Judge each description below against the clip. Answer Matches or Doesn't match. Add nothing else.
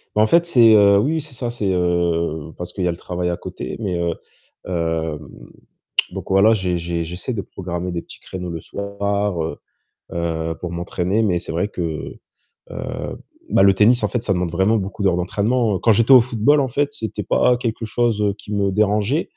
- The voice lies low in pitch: Matches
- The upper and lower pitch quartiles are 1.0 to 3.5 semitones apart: Doesn't match